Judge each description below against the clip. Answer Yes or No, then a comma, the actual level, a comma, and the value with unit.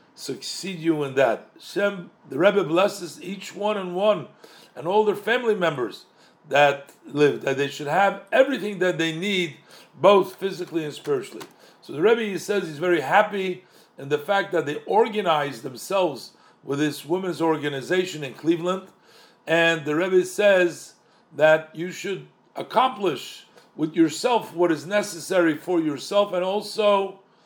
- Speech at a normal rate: Yes, average, 150 wpm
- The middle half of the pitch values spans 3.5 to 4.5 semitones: Yes, average, 3.9 semitones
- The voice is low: No, medium, 180 Hz